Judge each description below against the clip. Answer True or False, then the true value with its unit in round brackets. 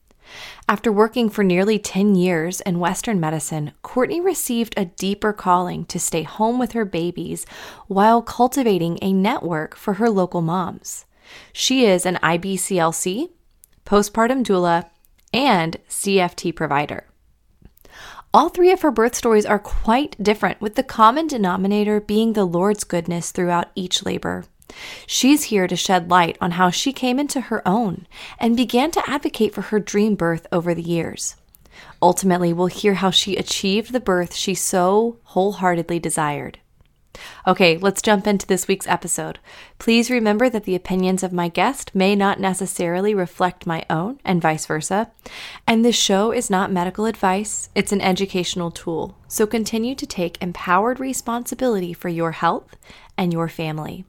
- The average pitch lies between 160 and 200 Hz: True (190 Hz)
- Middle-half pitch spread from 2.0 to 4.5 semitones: True (4.1 semitones)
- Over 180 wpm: False (155 wpm)